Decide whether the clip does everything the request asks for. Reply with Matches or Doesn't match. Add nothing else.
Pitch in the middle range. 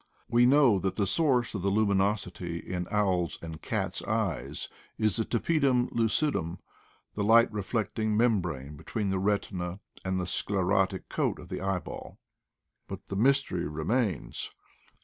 Doesn't match